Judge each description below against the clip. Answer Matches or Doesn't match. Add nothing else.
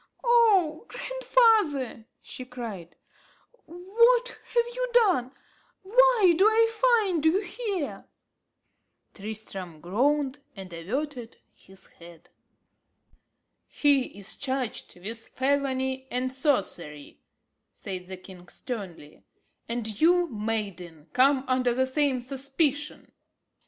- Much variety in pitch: Matches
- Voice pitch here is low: Doesn't match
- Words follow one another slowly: Matches